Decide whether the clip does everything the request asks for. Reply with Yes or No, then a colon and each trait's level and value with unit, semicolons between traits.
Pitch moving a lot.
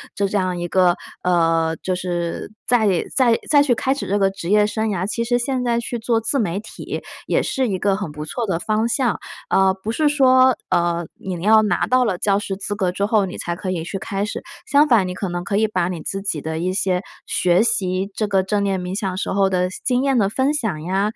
No: average, 3.9 semitones